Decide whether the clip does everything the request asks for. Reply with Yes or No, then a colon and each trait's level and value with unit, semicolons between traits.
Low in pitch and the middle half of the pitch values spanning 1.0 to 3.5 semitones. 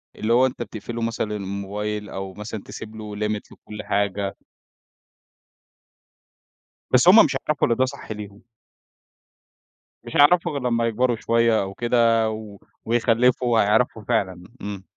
Yes: low, 110 Hz; narrow, 2.6 semitones